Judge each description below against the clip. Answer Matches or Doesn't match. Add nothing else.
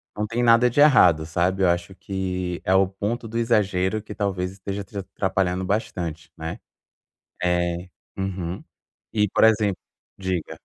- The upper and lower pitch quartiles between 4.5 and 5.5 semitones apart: Doesn't match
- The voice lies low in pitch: Matches